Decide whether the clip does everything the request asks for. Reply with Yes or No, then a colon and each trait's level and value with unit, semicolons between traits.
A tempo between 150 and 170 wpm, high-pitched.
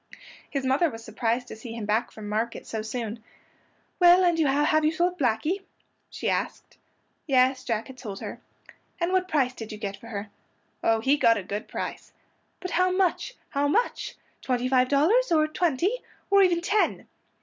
No: average, 180 wpm; very high, 265 Hz